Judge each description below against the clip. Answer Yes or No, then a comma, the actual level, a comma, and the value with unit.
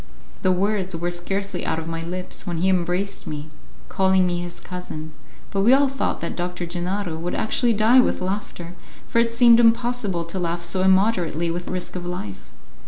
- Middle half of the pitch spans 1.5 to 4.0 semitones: Yes, average, 2.9 semitones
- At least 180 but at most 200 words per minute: Yes, average, 185 wpm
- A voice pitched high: No, medium, 180 Hz